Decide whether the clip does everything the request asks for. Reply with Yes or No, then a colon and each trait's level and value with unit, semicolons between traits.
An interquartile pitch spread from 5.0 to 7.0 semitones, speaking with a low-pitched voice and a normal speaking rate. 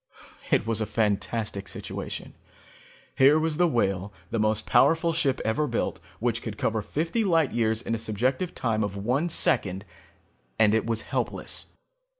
Yes: wide, 5.5 semitones; low, 115 Hz; average, 155 wpm